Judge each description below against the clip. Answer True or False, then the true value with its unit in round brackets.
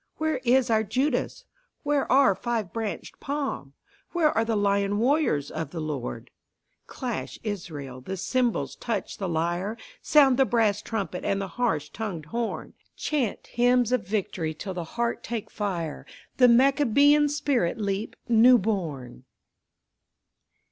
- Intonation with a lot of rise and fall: True (5.9 semitones)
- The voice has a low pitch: False (220 Hz)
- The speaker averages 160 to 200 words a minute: False (140 wpm)